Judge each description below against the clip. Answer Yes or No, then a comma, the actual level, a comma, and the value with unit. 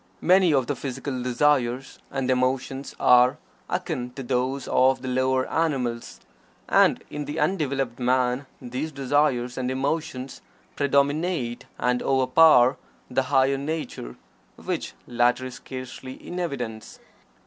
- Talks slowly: Yes, slow, 125 wpm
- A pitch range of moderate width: No, narrow, 2.3 semitones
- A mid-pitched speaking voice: No, low, 130 Hz